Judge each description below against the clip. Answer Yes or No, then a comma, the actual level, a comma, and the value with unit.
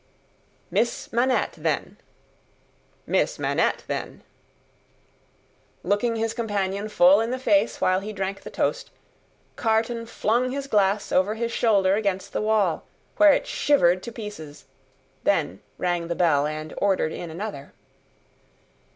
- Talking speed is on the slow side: Yes, slow, 130 wpm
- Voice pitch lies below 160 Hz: No, high, 205 Hz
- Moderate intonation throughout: Yes, average, 3.8 semitones